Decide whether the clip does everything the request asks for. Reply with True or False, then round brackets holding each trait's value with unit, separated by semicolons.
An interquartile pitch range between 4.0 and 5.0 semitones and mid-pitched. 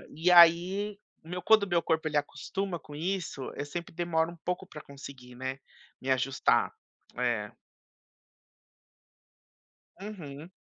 True (4.3 semitones; 160 Hz)